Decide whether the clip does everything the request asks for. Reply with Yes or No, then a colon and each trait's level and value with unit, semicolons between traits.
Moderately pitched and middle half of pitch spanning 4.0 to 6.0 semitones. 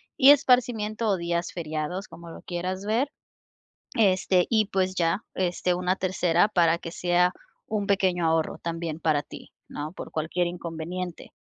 No: medium, 180 Hz; average, 2.8 semitones